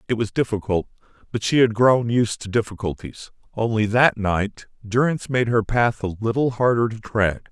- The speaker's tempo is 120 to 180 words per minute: Yes, average, 175 wpm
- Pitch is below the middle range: Yes, low, 110 Hz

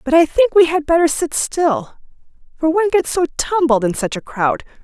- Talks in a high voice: Yes, very high, 295 Hz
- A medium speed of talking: No, fast, 210 wpm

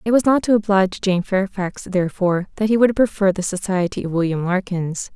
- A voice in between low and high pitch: No, high, 195 Hz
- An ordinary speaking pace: No, fast, 210 wpm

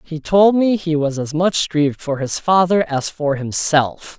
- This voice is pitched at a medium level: Yes, medium, 160 Hz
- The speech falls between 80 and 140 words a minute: No, average, 200 wpm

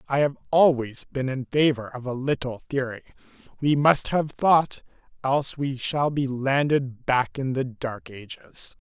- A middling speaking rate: Yes, average, 165 wpm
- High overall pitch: No, low, 135 Hz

